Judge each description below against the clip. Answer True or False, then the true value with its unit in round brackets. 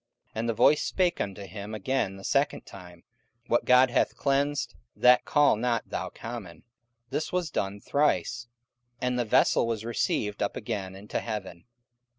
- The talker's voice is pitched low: True (115 Hz)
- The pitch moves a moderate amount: True (4.6 semitones)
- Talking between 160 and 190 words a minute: True (165 wpm)